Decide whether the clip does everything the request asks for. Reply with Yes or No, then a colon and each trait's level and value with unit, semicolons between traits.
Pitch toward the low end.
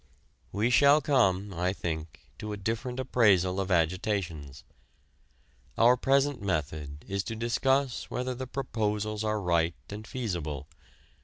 Yes: low, 105 Hz